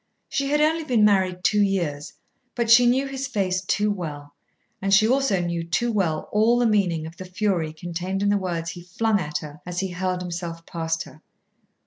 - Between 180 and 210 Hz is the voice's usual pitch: Yes, medium, 185 Hz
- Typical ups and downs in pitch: Yes, average, 4.2 semitones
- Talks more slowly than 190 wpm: No, average, 200 wpm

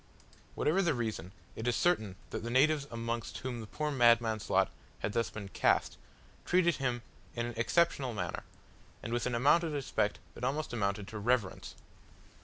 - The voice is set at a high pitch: No, low, 120 Hz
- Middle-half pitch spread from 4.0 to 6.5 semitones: Yes, average, 4.4 semitones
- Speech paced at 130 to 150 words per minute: No, average, 175 wpm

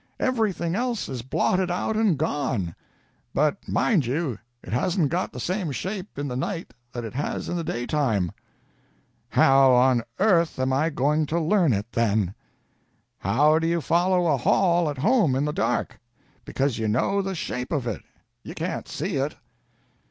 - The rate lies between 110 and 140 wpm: No, average, 170 wpm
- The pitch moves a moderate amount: No, wide, 5.8 semitones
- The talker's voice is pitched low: No, medium, 150 Hz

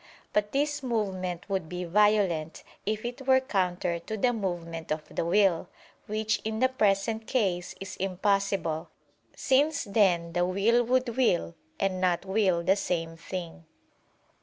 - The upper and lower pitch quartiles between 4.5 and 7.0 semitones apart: No, average, 3.9 semitones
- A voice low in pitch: No, high, 195 Hz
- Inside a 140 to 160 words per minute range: Yes, average, 145 wpm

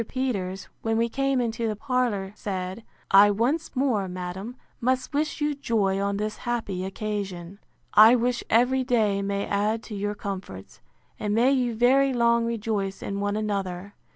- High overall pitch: Yes, high, 215 Hz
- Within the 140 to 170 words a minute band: Yes, average, 160 wpm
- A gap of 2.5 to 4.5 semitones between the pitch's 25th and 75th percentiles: Yes, average, 3.6 semitones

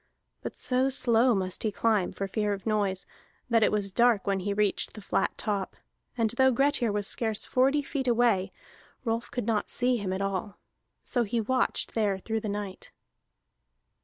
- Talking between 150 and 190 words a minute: Yes, average, 180 wpm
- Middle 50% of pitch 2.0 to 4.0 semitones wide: Yes, average, 3.3 semitones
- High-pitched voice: Yes, high, 215 Hz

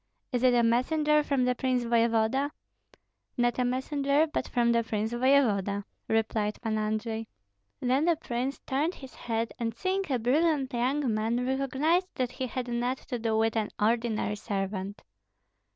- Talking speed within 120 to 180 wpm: Yes, average, 160 wpm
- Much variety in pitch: No, average, 3.3 semitones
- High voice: Yes, high, 245 Hz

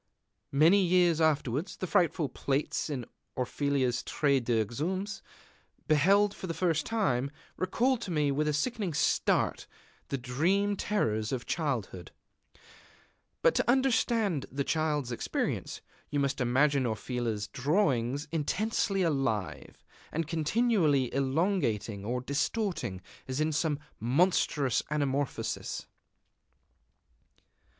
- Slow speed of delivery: Yes, slow, 110 wpm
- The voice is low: No, medium, 150 Hz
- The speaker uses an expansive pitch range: Yes, wide, 6.0 semitones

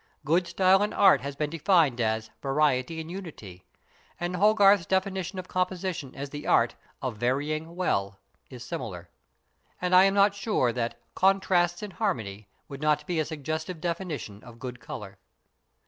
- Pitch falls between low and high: Yes, medium, 160 Hz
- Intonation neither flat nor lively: No, wide, 6.6 semitones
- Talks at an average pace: Yes, average, 160 wpm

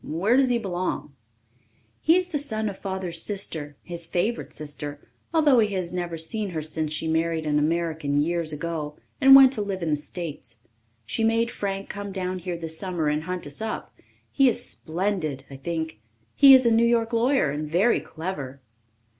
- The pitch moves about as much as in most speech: No, wide, 5.9 semitones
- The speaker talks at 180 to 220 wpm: Yes, average, 190 wpm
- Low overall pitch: No, medium, 175 Hz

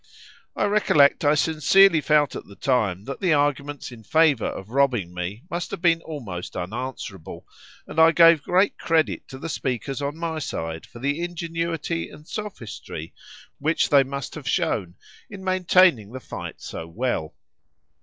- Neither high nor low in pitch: Yes, medium, 145 Hz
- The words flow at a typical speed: Yes, average, 160 wpm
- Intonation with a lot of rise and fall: Yes, wide, 5.8 semitones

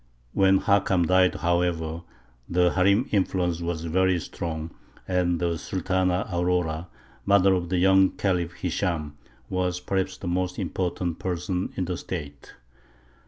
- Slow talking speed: Yes, slow, 130 wpm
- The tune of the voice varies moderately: No, narrow, 1.5 semitones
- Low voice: Yes, very low, 90 Hz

